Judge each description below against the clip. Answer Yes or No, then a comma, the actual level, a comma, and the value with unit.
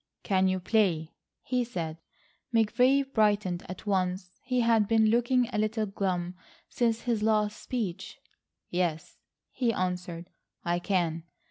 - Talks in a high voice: Yes, high, 205 Hz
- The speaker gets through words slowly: Yes, slow, 130 wpm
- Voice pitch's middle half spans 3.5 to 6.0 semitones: Yes, average, 4.1 semitones